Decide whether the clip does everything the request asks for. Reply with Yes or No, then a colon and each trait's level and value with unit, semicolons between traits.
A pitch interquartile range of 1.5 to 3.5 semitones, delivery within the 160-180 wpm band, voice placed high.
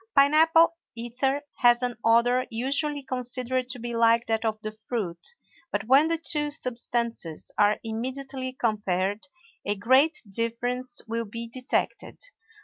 No: average, 2.8 semitones; average, 140 wpm; high, 245 Hz